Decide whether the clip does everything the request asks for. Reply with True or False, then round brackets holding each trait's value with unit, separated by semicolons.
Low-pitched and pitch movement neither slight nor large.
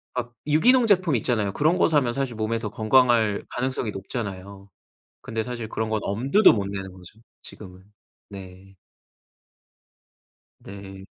True (110 Hz; 4.5 semitones)